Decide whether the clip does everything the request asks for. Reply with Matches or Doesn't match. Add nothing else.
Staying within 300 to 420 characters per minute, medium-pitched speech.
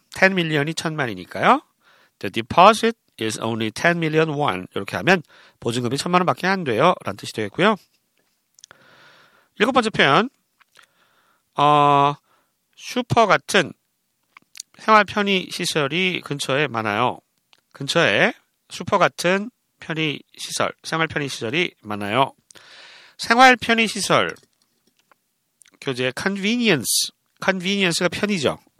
Doesn't match